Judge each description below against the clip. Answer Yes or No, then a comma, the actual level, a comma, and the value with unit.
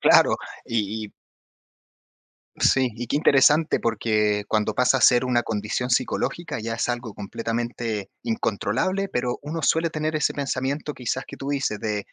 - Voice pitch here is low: Yes, low, 120 Hz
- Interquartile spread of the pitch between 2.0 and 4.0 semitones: No, average, 4.4 semitones